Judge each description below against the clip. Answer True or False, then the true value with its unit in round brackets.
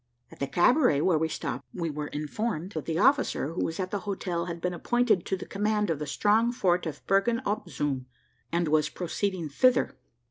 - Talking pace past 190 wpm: True (205 wpm)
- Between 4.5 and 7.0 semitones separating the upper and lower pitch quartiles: True (5.0 semitones)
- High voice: False (175 Hz)